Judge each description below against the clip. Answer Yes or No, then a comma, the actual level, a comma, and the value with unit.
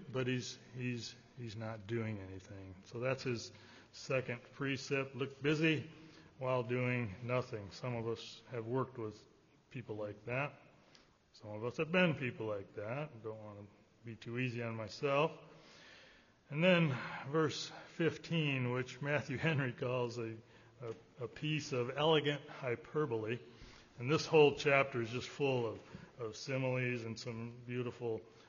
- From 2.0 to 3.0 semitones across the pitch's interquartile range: No, average, 3.7 semitones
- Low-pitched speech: Yes, low, 125 Hz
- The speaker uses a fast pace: No, average, 150 wpm